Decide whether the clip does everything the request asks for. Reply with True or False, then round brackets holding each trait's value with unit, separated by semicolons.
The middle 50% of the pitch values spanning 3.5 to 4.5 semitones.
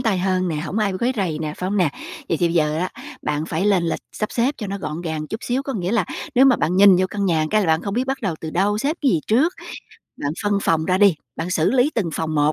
False (4.9 semitones)